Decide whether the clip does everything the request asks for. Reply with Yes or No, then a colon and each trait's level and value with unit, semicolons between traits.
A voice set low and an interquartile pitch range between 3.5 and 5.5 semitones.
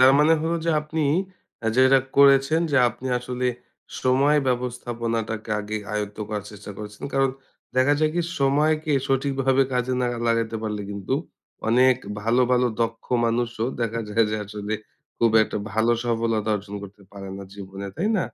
Yes: low, 120 Hz; average, 3.8 semitones